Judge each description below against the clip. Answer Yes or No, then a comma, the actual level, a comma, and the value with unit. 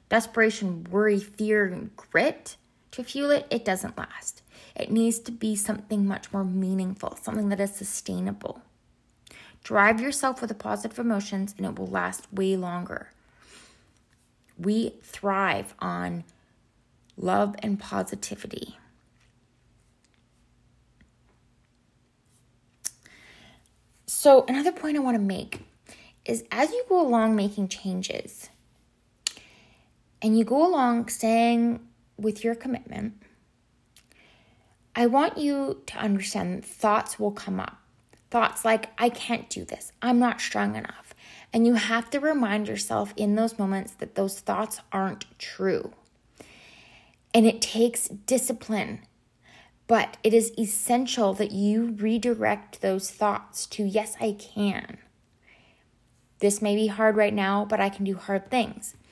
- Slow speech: Yes, slow, 125 wpm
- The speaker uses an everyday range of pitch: Yes, average, 3.0 semitones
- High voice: Yes, high, 210 Hz